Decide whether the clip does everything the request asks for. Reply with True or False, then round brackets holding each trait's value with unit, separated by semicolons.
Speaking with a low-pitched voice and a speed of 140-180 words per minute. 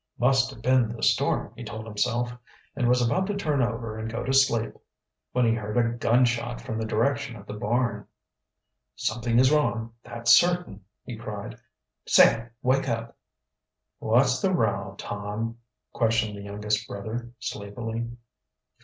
True (115 Hz; 155 wpm)